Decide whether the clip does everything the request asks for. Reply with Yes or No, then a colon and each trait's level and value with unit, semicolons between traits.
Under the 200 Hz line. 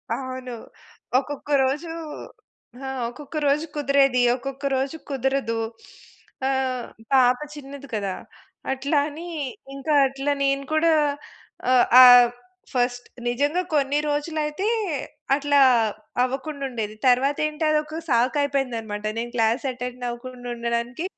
No: very high, 270 Hz